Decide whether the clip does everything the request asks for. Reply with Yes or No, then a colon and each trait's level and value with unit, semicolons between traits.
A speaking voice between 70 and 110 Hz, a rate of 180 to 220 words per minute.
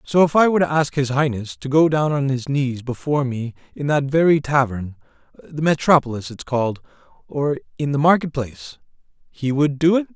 No: medium, 140 Hz; average, 185 wpm